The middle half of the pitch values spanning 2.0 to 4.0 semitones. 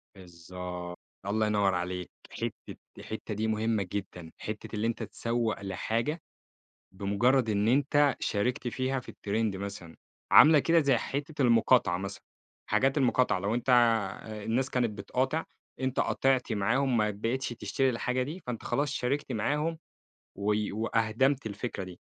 No: average, 4.6 semitones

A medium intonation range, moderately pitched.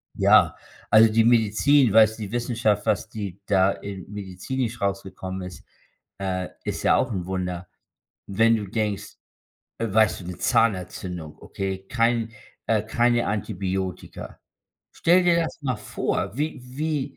No: average, 3.8 semitones; low, 105 Hz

